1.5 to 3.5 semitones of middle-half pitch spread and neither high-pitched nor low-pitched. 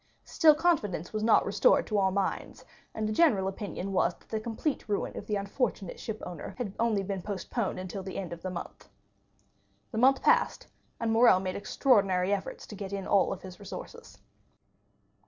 No: average, 3.1 semitones; high, 200 Hz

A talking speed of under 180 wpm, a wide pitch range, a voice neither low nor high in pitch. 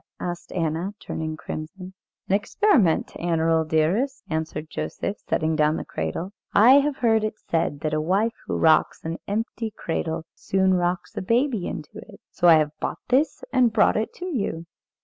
Yes: average, 170 wpm; wide, 5.7 semitones; medium, 180 Hz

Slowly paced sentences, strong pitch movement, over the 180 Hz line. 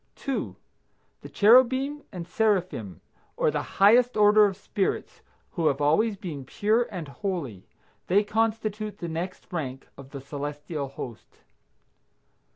Yes: slow, 130 wpm; wide, 6.6 semitones; high, 190 Hz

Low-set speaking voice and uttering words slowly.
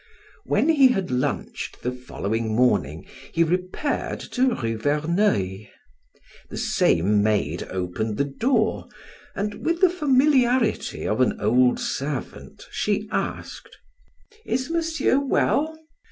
No: medium, 165 Hz; slow, 115 wpm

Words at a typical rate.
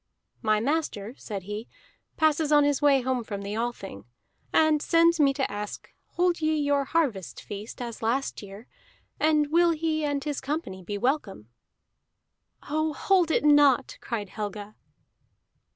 Yes: average, 150 wpm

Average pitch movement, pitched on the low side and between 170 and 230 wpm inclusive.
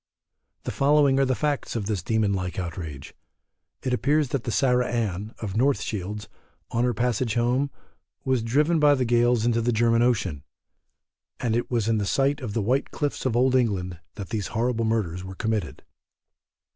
Yes: average, 3.6 semitones; low, 115 Hz; average, 180 wpm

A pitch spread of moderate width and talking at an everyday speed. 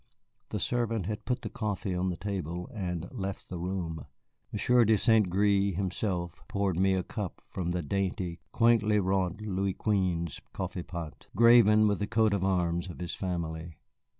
Yes: average, 3.1 semitones; average, 165 wpm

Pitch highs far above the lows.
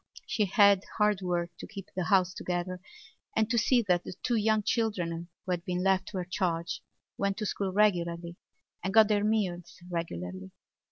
No: average, 3.2 semitones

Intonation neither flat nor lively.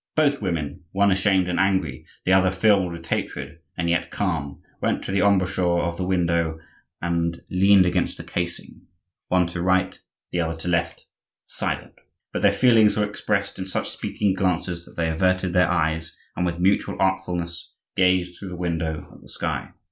No: narrow, 2.0 semitones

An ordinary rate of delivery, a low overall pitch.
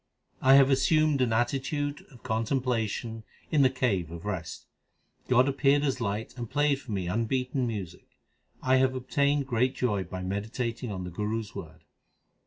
Yes: average, 165 wpm; low, 125 Hz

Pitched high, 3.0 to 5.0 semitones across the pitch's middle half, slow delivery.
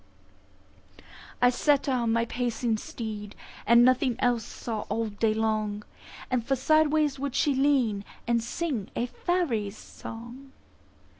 Yes: high, 235 Hz; average, 3.6 semitones; slow, 130 wpm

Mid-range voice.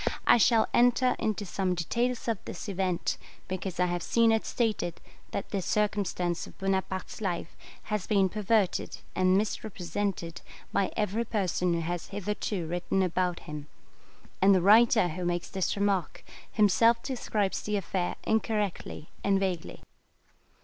No: high, 195 Hz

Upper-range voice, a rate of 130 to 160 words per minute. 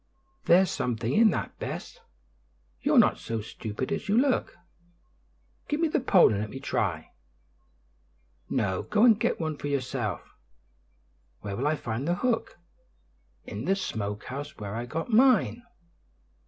No: medium, 140 Hz; average, 150 wpm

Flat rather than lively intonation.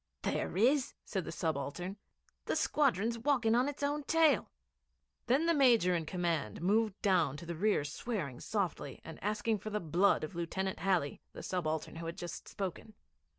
No: wide, 5.6 semitones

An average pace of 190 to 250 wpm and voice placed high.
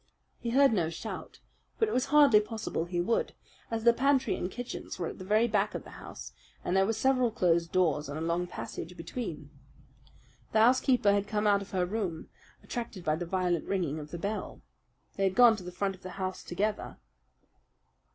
Yes: average, 200 wpm; high, 195 Hz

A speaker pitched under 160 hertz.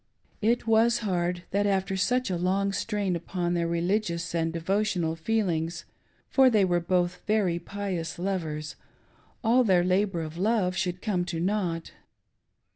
No: medium, 185 Hz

